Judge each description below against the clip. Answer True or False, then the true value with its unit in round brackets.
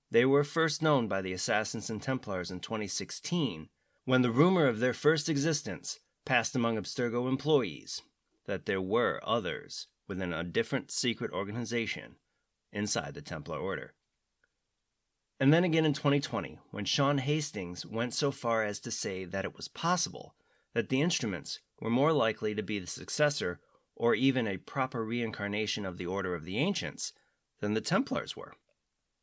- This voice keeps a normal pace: True (160 wpm)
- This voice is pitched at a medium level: False (120 Hz)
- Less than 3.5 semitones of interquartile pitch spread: False (5.3 semitones)